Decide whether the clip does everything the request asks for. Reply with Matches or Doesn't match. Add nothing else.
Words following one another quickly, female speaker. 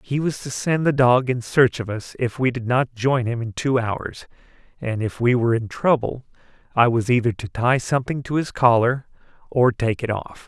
Doesn't match